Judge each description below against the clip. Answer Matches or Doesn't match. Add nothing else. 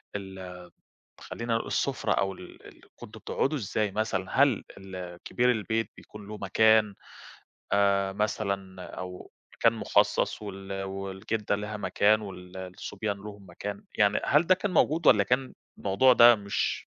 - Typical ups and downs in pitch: Doesn't match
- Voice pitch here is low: Matches